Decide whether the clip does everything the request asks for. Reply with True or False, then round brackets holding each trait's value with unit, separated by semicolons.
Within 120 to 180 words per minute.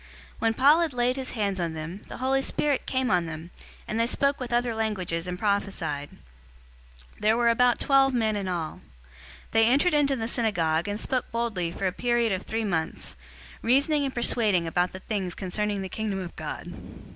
False (200 wpm)